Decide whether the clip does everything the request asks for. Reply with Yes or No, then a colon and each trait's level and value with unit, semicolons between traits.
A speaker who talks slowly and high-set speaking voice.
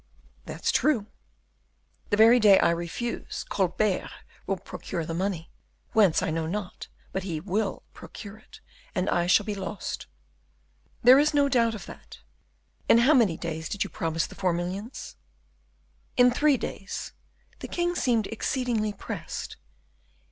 No: average, 150 wpm; high, 205 Hz